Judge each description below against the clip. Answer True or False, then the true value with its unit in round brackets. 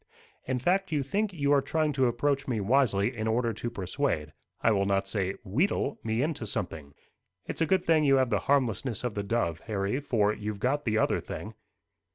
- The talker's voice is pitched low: True (120 Hz)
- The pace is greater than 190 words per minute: True (205 wpm)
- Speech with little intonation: False (5.6 semitones)